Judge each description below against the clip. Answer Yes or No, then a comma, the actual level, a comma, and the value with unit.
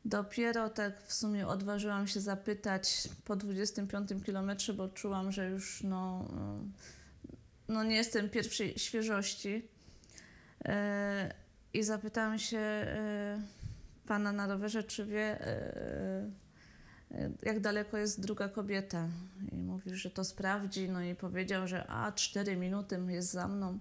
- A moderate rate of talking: Yes, average, 120 wpm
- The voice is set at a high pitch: Yes, high, 200 Hz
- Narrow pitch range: Yes, narrow, 1.9 semitones